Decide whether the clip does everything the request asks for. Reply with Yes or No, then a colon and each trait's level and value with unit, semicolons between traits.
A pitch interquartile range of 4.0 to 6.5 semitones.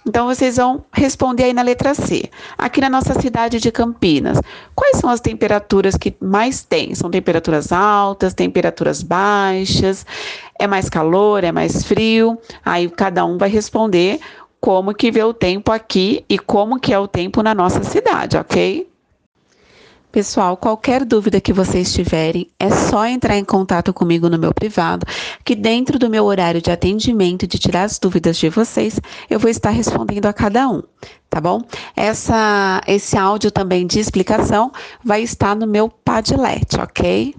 No: average, 3.6 semitones